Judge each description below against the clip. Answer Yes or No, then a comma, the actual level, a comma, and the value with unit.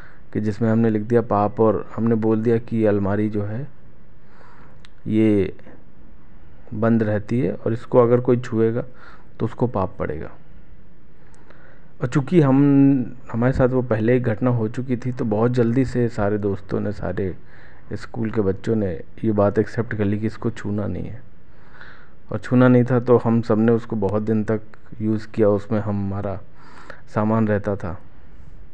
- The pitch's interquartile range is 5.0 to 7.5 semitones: No, average, 2.7 semitones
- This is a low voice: Yes, low, 110 Hz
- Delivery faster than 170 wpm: No, average, 165 wpm